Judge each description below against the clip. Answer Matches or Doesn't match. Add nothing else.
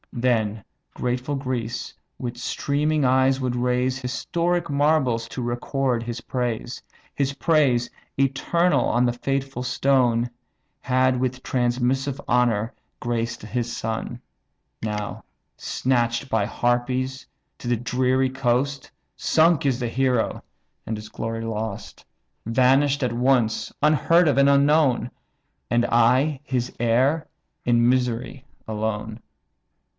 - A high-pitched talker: Doesn't match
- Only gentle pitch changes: Matches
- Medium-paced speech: Doesn't match